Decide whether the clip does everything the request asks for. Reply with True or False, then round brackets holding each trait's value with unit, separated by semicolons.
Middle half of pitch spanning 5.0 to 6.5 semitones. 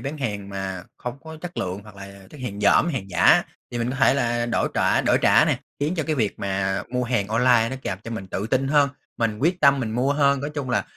True (5.5 semitones)